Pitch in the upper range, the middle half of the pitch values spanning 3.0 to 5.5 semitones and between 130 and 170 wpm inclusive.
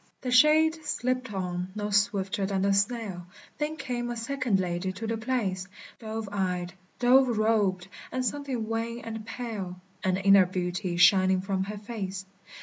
Yes: high, 210 Hz; average, 4.2 semitones; average, 155 wpm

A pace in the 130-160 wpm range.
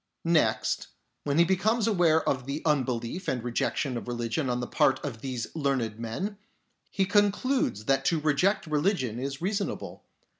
Yes: average, 155 wpm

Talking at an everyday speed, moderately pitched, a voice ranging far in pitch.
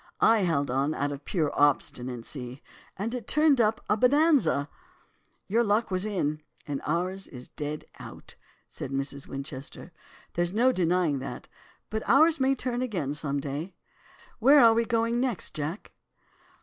Yes: average, 150 wpm; medium, 180 Hz; wide, 8.4 semitones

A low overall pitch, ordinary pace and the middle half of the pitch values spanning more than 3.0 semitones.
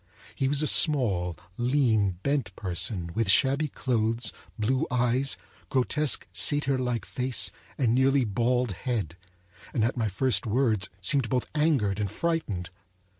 No: low, 125 Hz; slow, 130 wpm; average, 4.4 semitones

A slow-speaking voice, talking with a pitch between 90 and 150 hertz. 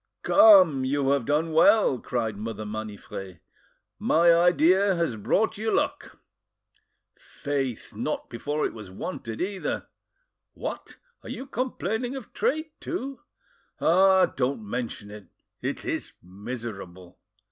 Yes: slow, 120 wpm; medium, 140 Hz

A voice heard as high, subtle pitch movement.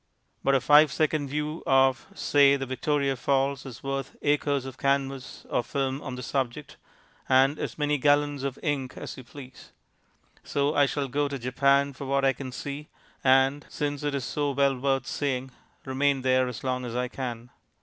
No: low, 135 Hz; narrow, 1.6 semitones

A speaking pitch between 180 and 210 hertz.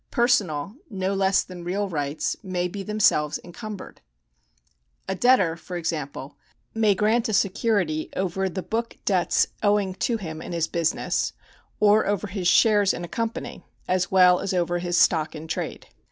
Yes: medium, 185 Hz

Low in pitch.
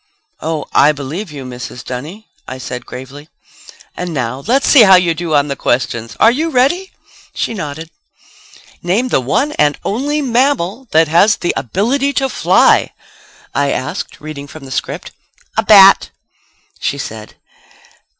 No: medium, 165 Hz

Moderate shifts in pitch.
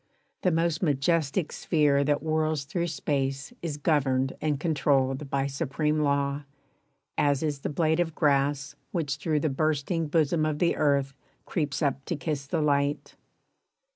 No: narrow, 2.2 semitones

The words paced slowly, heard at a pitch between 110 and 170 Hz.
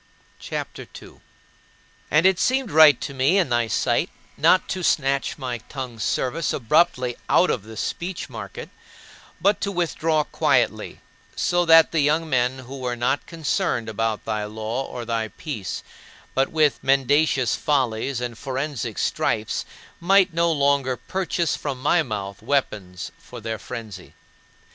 No: average, 150 wpm; low, 135 Hz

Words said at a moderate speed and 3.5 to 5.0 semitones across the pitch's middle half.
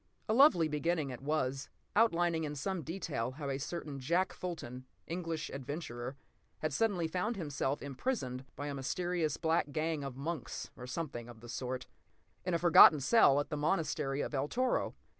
Yes: average, 170 wpm; average, 4.3 semitones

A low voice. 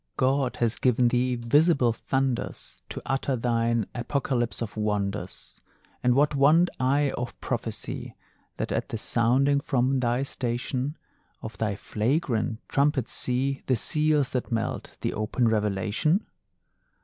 Yes: low, 125 Hz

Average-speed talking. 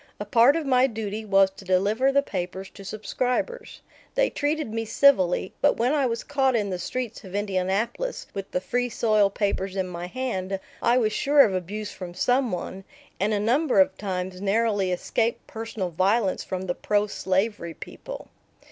Yes: average, 180 wpm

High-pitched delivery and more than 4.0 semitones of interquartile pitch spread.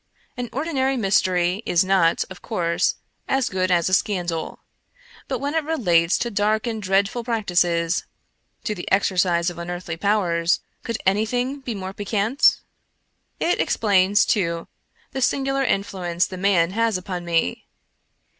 Yes: high, 195 Hz; average, 4.6 semitones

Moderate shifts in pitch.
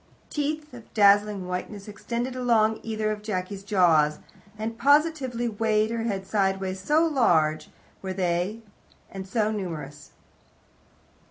Yes: average, 3.7 semitones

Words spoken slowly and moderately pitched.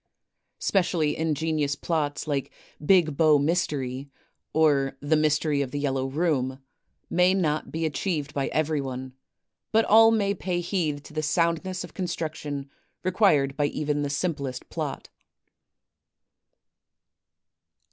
Yes: slow, 125 wpm; medium, 155 Hz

